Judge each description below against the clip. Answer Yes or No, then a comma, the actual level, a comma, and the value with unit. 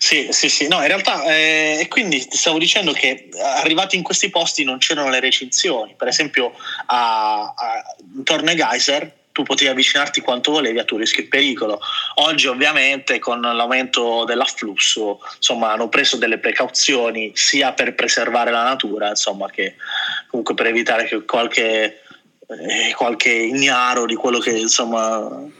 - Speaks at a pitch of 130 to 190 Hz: Yes, medium, 140 Hz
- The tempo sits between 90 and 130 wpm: No, average, 150 wpm